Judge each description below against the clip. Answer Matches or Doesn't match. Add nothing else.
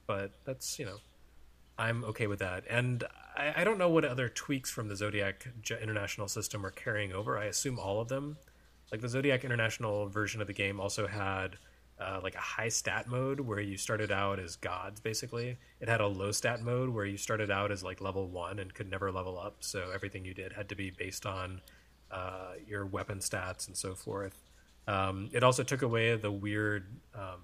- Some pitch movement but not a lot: Matches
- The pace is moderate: Doesn't match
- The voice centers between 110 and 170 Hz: Doesn't match